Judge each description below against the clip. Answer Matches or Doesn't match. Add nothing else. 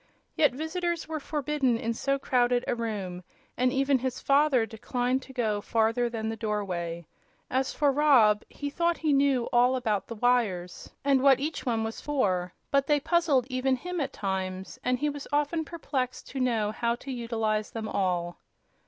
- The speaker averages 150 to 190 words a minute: Matches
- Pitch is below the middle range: Doesn't match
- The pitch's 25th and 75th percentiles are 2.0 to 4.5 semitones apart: Matches